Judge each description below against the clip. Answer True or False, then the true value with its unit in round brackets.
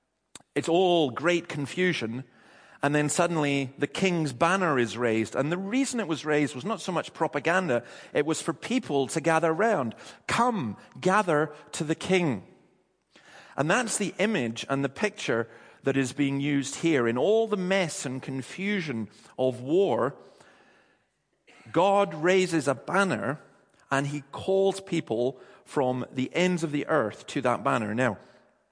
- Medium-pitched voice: True (155 Hz)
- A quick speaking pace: False (155 wpm)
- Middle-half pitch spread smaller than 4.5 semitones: False (5.2 semitones)